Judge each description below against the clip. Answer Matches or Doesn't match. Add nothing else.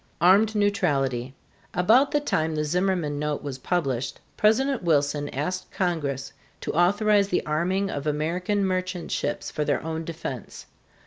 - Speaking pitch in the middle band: Matches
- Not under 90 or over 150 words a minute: Matches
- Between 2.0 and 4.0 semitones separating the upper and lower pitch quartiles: Doesn't match